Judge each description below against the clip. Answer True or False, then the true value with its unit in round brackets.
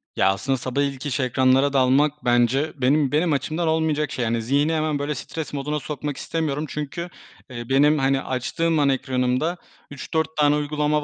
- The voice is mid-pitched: True (145 Hz)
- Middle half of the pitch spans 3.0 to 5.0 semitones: False (2.5 semitones)